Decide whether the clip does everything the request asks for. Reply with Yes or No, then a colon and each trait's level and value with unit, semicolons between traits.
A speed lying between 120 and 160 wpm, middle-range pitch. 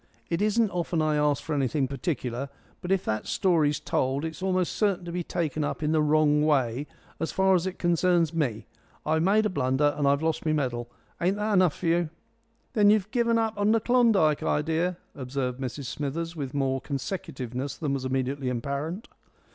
No: average, 185 wpm; medium, 155 Hz